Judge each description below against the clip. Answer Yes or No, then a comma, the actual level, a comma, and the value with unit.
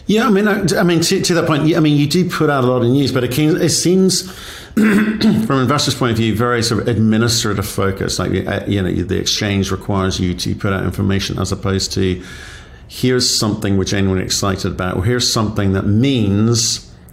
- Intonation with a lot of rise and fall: Yes, wide, 7.4 semitones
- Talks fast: Yes, fast, 215 wpm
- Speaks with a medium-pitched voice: No, low, 115 Hz